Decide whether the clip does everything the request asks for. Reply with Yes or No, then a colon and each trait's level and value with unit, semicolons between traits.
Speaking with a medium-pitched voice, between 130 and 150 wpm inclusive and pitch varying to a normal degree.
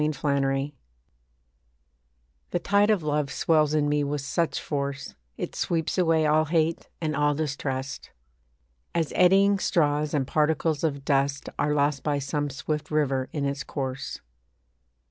No: medium, 150 Hz; average, 145 wpm; narrow, 2.0 semitones